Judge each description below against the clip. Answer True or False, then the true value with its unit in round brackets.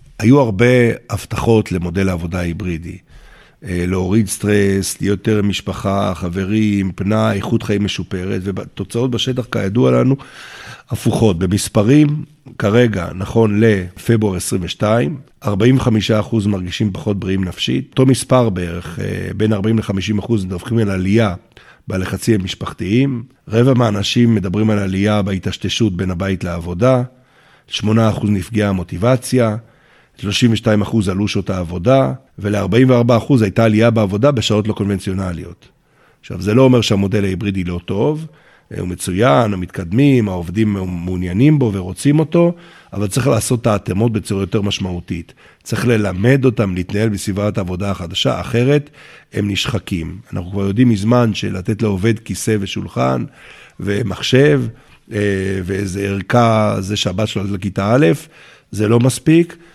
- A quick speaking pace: False (125 wpm)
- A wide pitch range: False (3.6 semitones)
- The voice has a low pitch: True (105 Hz)